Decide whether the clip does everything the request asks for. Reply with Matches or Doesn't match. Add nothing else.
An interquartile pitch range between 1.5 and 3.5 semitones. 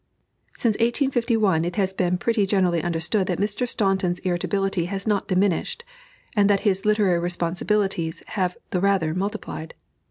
Matches